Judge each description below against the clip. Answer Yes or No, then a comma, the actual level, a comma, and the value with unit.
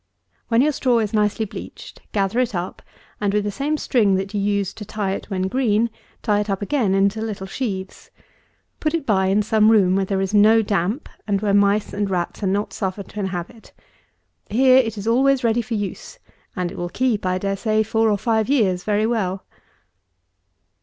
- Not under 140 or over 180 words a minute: No, average, 200 wpm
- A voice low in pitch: No, high, 210 Hz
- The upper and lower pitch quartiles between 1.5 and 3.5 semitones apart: Yes, narrow, 2.5 semitones